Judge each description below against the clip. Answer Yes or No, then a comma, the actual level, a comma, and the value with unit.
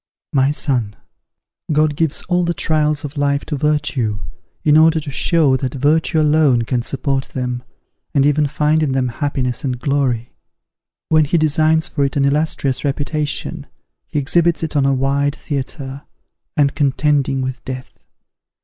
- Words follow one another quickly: No, average, 155 wpm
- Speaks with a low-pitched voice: No, medium, 145 Hz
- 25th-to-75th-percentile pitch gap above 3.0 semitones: No, narrow, 2.4 semitones